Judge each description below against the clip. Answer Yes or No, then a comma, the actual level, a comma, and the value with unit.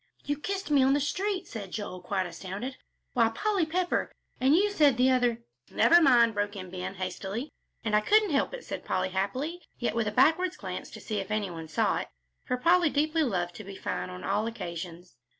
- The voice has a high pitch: Yes, high, 235 Hz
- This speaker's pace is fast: Yes, fast, 215 wpm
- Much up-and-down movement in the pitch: Yes, wide, 8.3 semitones